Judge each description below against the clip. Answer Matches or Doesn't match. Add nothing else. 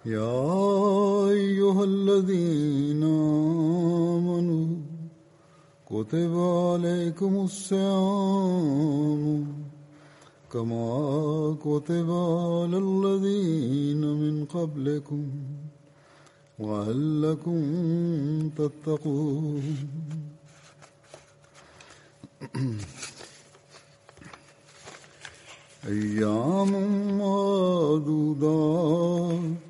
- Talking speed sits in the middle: Doesn't match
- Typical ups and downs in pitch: Matches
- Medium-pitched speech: Matches